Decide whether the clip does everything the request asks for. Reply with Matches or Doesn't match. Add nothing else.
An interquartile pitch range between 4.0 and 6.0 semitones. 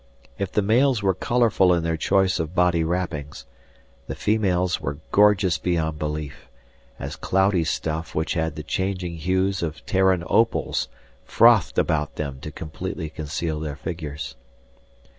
Doesn't match